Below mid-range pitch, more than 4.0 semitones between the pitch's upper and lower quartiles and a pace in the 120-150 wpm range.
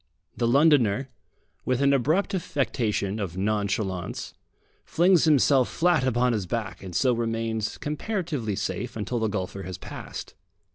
Yes: low, 120 Hz; wide, 5.6 semitones; slow, 135 wpm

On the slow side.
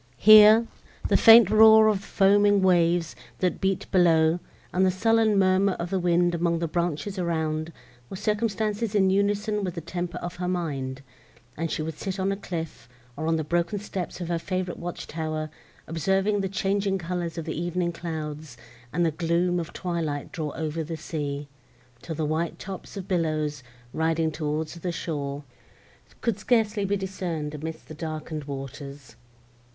No: average, 165 wpm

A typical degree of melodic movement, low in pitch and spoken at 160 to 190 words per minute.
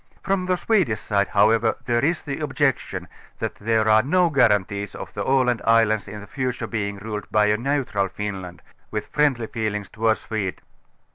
Yes: average, 4.4 semitones; low, 110 Hz; average, 165 wpm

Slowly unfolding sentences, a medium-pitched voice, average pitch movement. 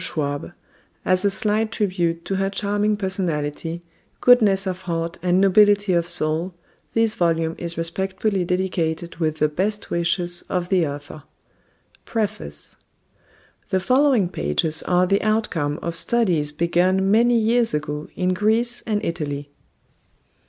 Yes: slow, 130 wpm; medium, 180 Hz; average, 3.8 semitones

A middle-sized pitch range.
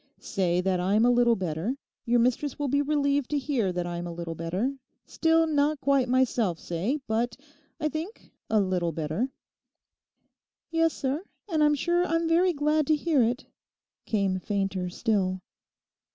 No: wide, 8.1 semitones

